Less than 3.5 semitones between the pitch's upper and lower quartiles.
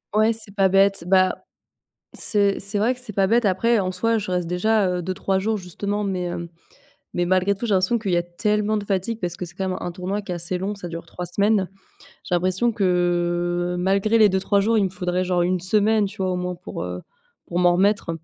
Yes: average, 2.7 semitones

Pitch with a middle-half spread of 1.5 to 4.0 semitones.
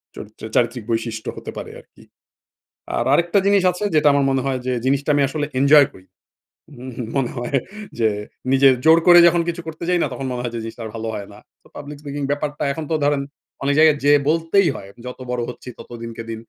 No: average, 4.4 semitones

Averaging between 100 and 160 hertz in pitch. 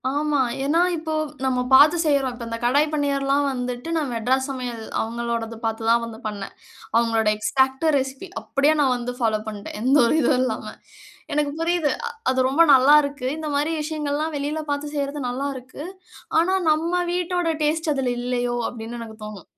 No: very high, 270 Hz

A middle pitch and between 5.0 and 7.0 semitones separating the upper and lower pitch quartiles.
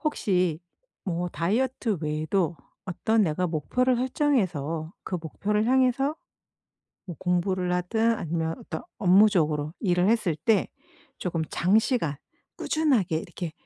Yes: medium, 180 Hz; average, 5.3 semitones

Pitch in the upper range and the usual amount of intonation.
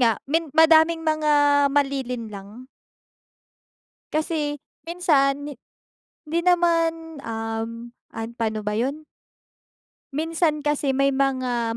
Yes: very high, 285 Hz; average, 4.9 semitones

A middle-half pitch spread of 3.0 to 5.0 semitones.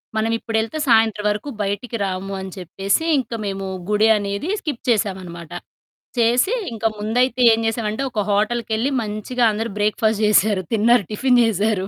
No: narrow, 2.6 semitones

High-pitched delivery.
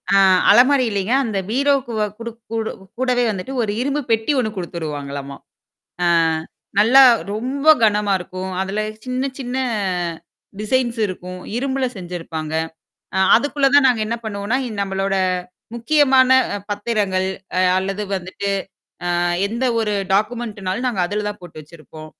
Yes: high, 215 Hz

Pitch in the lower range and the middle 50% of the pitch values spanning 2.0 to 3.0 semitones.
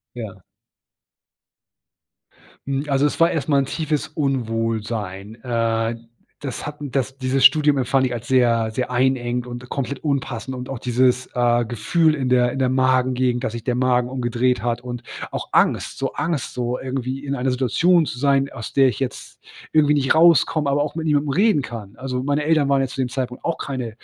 Yes: low, 130 Hz; narrow, 2.5 semitones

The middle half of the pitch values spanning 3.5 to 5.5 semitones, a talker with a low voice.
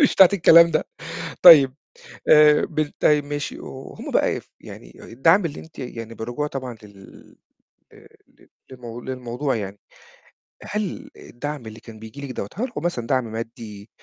Yes: average, 4.8 semitones; low, 130 Hz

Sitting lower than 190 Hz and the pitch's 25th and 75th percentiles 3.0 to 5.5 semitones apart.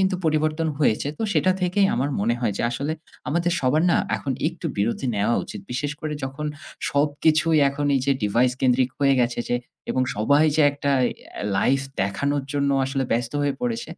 Yes: medium, 140 Hz; average, 3.6 semitones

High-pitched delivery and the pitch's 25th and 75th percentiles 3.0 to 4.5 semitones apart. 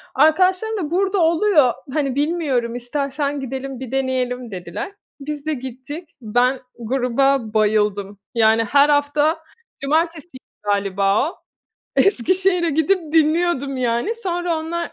No: very high, 280 Hz; average, 5.1 semitones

